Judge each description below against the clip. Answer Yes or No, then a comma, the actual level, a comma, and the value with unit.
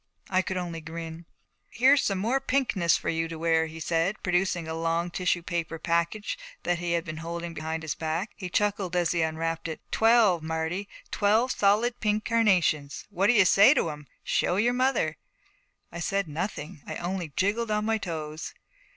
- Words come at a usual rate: Yes, average, 185 wpm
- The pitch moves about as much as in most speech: Yes, average, 4.1 semitones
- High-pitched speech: No, medium, 175 Hz